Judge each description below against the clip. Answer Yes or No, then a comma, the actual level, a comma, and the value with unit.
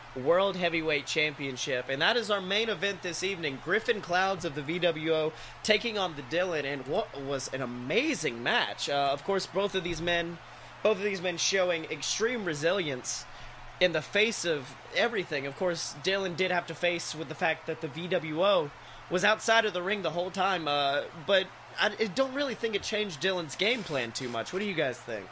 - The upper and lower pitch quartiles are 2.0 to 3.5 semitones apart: No, average, 5.1 semitones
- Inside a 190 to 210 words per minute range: Yes, average, 200 wpm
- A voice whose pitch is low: No, medium, 175 Hz